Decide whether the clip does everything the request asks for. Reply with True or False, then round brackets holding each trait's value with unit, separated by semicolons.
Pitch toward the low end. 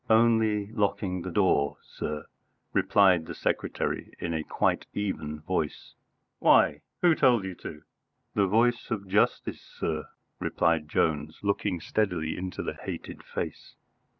True (95 Hz)